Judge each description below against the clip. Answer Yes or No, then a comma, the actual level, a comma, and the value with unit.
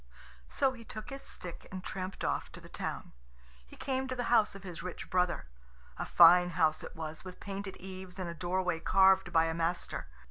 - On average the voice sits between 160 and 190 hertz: Yes, medium, 185 Hz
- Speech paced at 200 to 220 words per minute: Yes, fast, 205 wpm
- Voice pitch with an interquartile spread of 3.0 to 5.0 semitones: No, narrow, 2.4 semitones